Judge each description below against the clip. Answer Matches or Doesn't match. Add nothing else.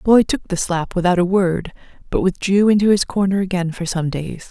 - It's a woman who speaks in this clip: Matches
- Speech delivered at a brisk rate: Matches